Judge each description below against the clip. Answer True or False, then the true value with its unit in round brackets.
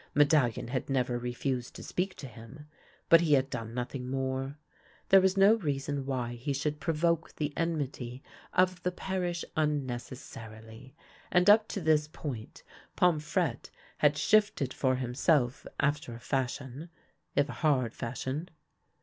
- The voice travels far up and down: False (4.5 semitones)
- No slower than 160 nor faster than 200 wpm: False (150 wpm)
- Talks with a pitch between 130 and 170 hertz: True (140 Hz)